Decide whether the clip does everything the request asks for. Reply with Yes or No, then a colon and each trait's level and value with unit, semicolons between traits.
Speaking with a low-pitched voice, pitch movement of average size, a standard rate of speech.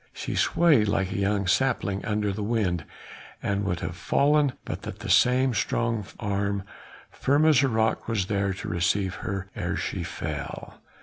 Yes: low, 105 Hz; average, 3.8 semitones; average, 170 wpm